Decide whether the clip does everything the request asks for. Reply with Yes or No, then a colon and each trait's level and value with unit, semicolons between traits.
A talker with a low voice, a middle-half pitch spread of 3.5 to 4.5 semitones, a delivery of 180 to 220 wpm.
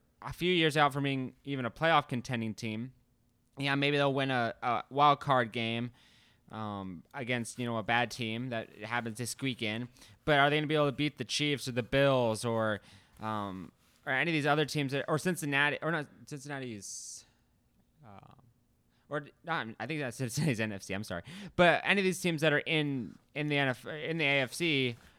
Yes: low, 130 Hz; average, 4.1 semitones; average, 200 wpm